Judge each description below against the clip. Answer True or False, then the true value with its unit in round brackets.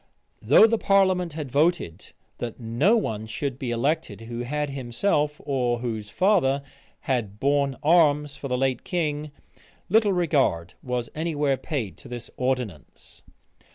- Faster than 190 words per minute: False (145 wpm)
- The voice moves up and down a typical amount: True (4.7 semitones)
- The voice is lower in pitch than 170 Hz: True (140 Hz)